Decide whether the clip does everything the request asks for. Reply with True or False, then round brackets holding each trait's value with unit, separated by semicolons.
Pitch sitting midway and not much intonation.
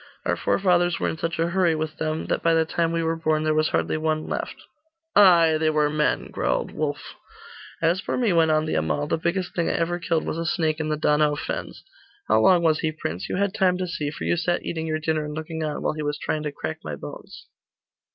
True (160 Hz; 1.7 semitones)